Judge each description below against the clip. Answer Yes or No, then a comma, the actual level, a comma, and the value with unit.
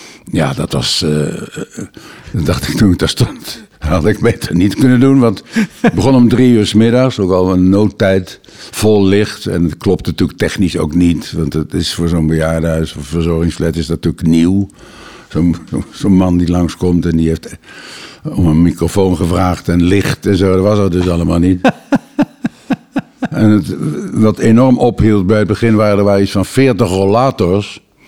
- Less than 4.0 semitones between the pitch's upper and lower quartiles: No, average, 4.7 semitones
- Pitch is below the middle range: Yes, very low, 95 Hz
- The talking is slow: No, average, 185 wpm